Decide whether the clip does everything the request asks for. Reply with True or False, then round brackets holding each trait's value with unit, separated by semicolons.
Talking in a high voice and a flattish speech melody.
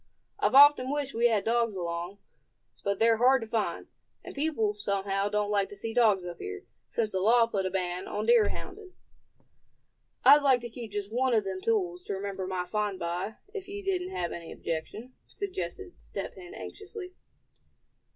False (220 Hz; 5.3 semitones)